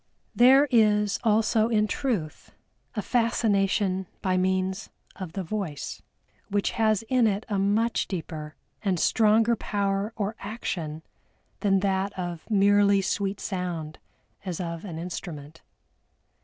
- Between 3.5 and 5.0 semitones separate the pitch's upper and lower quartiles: No, average, 2.9 semitones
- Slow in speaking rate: Yes, slow, 125 wpm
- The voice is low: No, high, 200 Hz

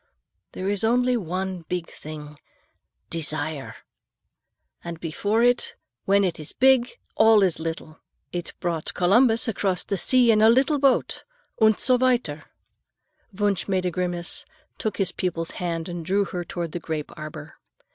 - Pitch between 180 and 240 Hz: Yes, medium, 185 Hz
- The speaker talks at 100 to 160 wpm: Yes, average, 145 wpm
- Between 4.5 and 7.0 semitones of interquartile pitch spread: Yes, average, 5.0 semitones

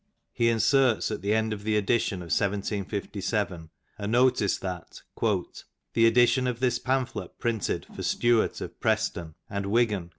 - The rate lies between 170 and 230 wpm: No, average, 145 wpm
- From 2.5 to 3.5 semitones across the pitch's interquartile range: Yes, average, 3.1 semitones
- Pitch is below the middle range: Yes, low, 110 Hz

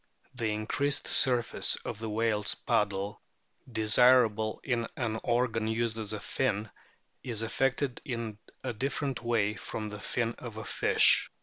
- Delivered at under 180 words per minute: Yes, average, 140 wpm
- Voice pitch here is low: Yes, low, 115 Hz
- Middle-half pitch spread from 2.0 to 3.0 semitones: Yes, narrow, 2.4 semitones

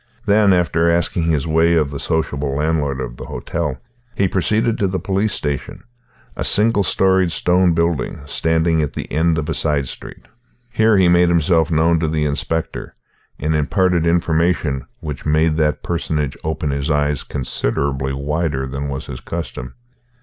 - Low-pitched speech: Yes, very low, 80 Hz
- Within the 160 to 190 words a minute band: Yes, average, 165 wpm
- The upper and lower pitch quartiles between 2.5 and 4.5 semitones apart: Yes, average, 3.0 semitones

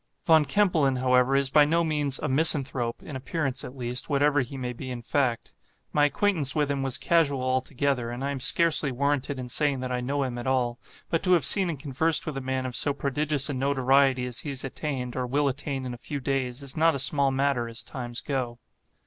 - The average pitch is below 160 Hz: Yes, low, 135 Hz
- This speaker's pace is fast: Yes, fast, 225 wpm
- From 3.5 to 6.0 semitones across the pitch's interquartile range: No, narrow, 2.4 semitones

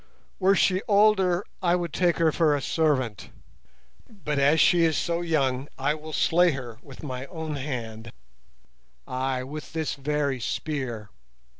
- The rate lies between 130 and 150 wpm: Yes, average, 145 wpm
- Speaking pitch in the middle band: Yes, medium, 150 Hz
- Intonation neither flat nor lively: Yes, average, 4.6 semitones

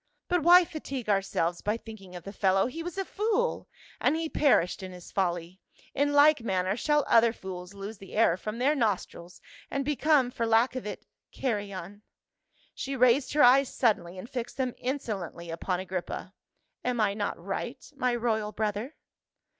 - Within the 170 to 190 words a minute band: Yes, average, 180 wpm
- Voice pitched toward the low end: No, high, 225 Hz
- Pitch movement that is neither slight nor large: No, wide, 6.1 semitones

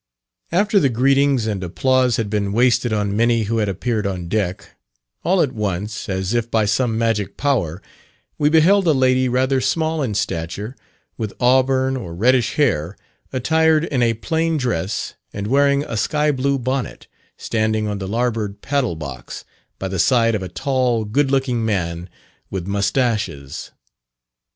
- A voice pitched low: Yes, low, 115 Hz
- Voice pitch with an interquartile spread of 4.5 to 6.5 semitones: Yes, average, 4.8 semitones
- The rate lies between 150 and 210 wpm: Yes, average, 160 wpm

